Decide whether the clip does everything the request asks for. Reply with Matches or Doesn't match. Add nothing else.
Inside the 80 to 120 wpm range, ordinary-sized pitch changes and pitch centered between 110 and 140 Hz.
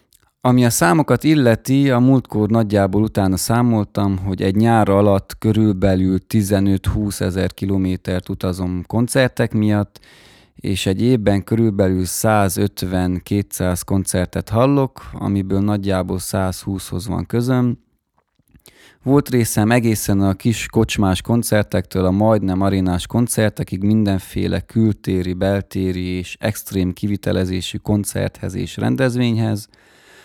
Doesn't match